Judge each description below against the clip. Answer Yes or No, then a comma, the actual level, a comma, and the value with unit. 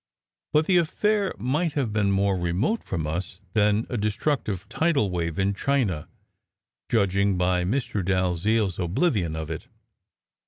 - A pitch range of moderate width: No, wide, 6.1 semitones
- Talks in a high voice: No, low, 100 Hz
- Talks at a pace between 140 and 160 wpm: Yes, average, 150 wpm